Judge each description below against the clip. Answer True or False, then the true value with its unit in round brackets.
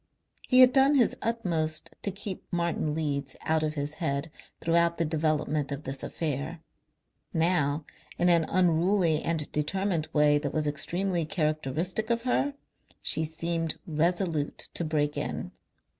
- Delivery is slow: False (145 wpm)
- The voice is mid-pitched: True (160 Hz)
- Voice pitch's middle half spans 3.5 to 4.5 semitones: False (3.0 semitones)